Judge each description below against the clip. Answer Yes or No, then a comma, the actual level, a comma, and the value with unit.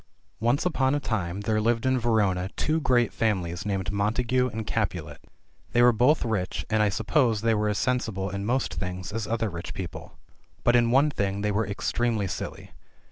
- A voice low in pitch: Yes, low, 110 Hz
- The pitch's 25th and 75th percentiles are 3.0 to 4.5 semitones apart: Yes, average, 3.5 semitones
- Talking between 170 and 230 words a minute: Yes, average, 190 wpm